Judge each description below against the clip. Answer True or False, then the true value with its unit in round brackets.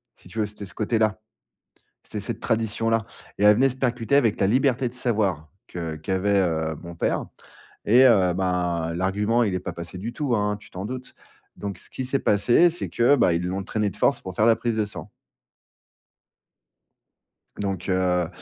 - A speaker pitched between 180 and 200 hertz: False (105 Hz)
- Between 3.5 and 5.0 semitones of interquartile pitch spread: True (4.3 semitones)